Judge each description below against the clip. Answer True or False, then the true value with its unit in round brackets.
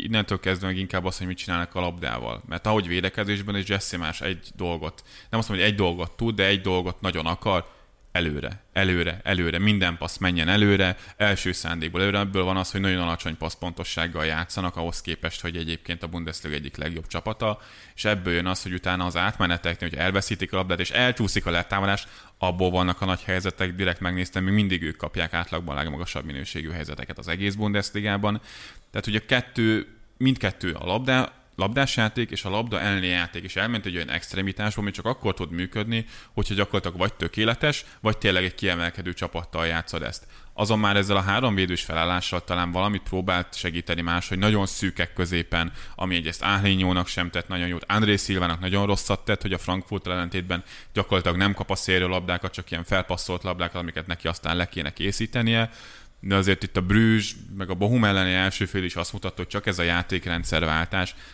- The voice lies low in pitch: True (95 Hz)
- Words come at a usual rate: False (190 wpm)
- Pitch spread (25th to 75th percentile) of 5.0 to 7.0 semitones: False (2.7 semitones)